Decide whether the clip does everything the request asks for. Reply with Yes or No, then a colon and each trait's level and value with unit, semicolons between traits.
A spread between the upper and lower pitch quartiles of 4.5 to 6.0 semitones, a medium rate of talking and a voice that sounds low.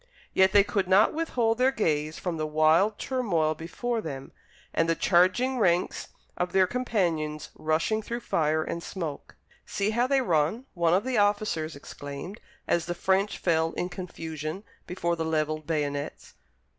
No: average, 5.1 semitones; average, 155 wpm; medium, 175 Hz